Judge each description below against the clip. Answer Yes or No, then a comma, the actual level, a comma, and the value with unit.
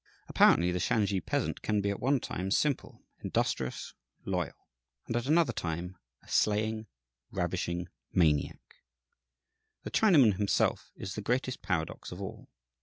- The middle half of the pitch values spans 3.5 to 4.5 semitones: No, average, 5.1 semitones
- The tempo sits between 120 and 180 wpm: Yes, slow, 135 wpm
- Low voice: Yes, low, 100 Hz